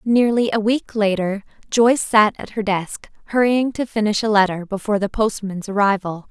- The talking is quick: No, average, 170 wpm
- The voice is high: Yes, high, 210 Hz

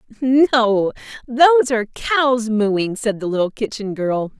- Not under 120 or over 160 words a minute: Yes, slow, 135 wpm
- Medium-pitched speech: No, high, 235 Hz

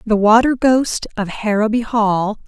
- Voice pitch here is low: No, high, 220 Hz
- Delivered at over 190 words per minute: No, average, 145 wpm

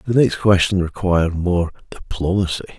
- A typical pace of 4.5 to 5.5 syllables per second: Yes, 5.1 syllables/s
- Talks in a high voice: No, very low, 90 Hz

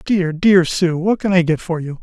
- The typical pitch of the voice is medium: Yes, medium, 175 Hz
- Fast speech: Yes, fast, 265 wpm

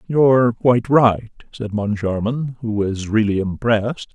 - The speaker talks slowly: Yes, slow, 130 wpm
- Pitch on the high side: No, low, 115 Hz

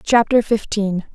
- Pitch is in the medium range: No, high, 215 Hz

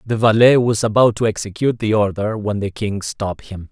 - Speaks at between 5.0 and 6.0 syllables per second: Yes, 5.5 syllables/s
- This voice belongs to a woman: No, male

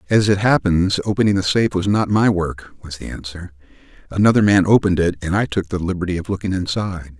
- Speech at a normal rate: No, fast, 210 wpm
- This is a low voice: Yes, very low, 95 Hz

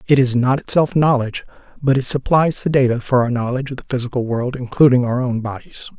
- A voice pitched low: Yes, low, 130 Hz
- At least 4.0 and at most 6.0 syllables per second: No, 6.2 syllables/s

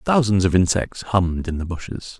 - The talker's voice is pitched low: Yes, very low, 95 Hz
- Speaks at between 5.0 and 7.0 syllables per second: Yes, 5.3 syllables/s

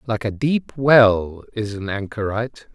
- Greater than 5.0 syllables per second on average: No, 4.0 syllables/s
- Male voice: Yes, male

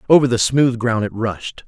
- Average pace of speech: No, fast, 215 wpm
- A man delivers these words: Yes, male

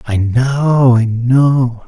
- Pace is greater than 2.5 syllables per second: No, 2.4 syllables/s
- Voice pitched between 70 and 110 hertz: No, low, 125 Hz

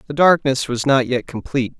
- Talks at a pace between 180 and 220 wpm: Yes, average, 200 wpm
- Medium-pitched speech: No, low, 130 Hz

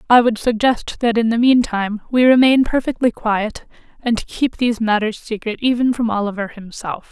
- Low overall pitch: No, high, 230 Hz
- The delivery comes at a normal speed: Yes, average, 170 wpm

